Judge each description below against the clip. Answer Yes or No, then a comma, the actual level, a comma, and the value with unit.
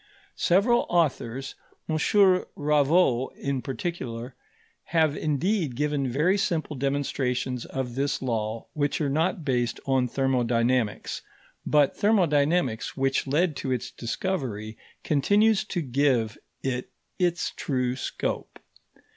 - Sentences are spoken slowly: Yes, slow, 110 wpm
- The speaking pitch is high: No, medium, 140 Hz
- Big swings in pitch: No, average, 4.7 semitones